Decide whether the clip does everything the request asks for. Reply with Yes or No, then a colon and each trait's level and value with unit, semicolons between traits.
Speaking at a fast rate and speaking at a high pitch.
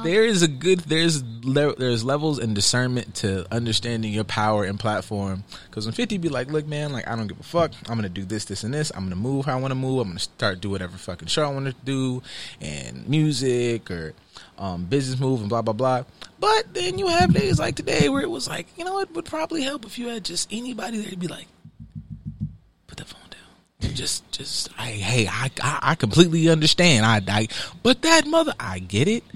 No: fast, 225 wpm; low, 130 Hz